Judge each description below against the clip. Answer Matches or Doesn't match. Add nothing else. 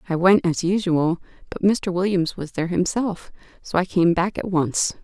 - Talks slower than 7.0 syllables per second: Matches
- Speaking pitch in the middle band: Matches